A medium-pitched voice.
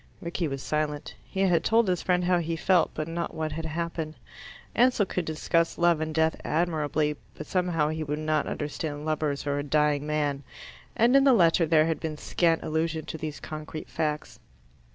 Yes: medium, 160 Hz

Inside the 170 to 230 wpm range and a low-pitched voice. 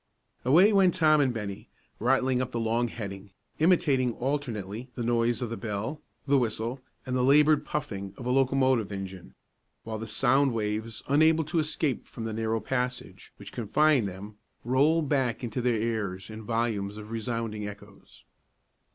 No: average, 160 wpm; low, 120 Hz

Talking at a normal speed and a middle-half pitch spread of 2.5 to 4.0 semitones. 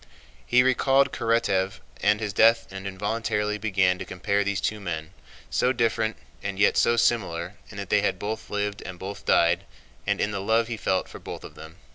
Yes: average, 195 wpm; average, 2.9 semitones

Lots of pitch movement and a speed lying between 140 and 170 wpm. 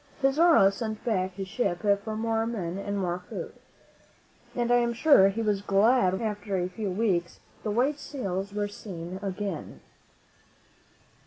No: average, 3.3 semitones; average, 155 wpm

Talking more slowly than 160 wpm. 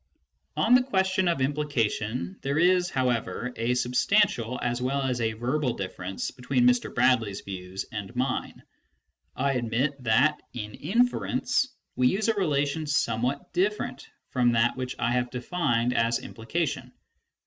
Yes: average, 140 wpm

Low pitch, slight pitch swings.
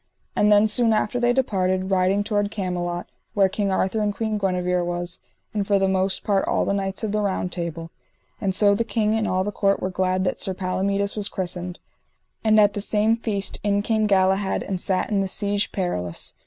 No: high, 195 Hz; narrow, 2.1 semitones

